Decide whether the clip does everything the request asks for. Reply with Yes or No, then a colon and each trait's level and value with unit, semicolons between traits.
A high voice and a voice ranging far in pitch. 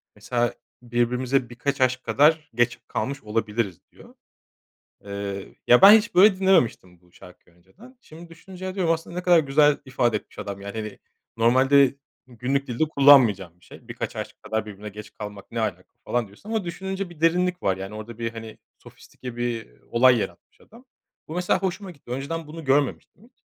No: low, 125 Hz; wide, 7.4 semitones